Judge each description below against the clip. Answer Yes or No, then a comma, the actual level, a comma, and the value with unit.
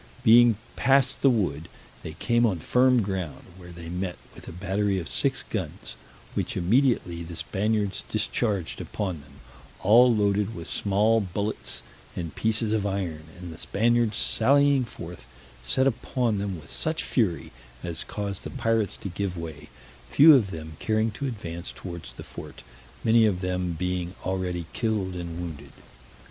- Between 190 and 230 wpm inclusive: No, average, 155 wpm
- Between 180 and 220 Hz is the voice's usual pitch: No, low, 100 Hz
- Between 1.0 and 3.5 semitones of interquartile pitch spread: No, average, 4.6 semitones